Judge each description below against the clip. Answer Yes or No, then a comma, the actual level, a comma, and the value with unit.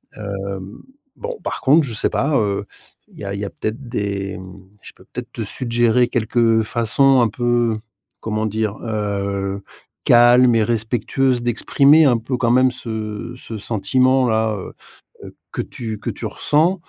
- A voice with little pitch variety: No, average, 3.2 semitones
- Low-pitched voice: Yes, low, 115 Hz